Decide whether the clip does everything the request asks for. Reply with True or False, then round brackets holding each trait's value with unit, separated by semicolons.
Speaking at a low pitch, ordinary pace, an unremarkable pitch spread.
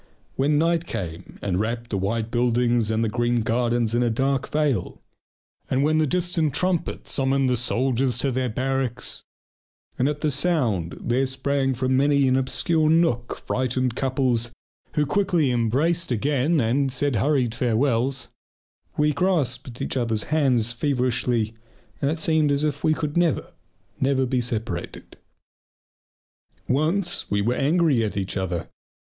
True (130 Hz; 150 wpm; 3.8 semitones)